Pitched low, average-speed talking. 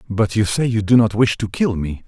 No: low, 110 Hz; fast, 290 wpm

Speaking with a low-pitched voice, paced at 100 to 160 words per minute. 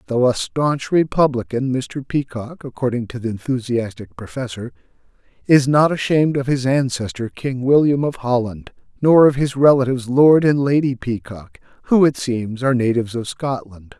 Yes: low, 130 Hz; average, 155 wpm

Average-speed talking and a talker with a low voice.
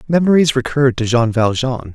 Yes: average, 155 wpm; low, 130 Hz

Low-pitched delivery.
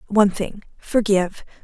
No: high, 200 Hz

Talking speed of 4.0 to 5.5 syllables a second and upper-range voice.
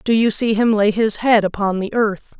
Yes: 4.9 syllables/s; high, 215 Hz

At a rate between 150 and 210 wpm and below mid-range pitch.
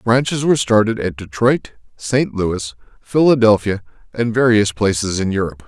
No: slow, 135 wpm; low, 110 Hz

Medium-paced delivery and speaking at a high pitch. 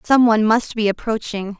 Yes: average, 190 wpm; high, 220 Hz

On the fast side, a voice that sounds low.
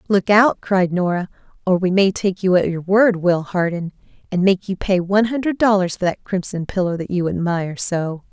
No: fast, 210 wpm; medium, 185 Hz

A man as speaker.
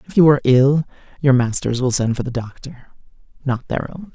Yes: male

